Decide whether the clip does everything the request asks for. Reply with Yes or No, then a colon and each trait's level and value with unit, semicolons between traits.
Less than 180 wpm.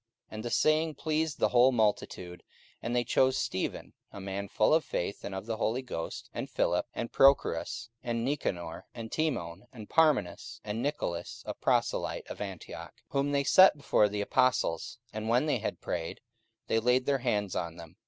No: average, 185 wpm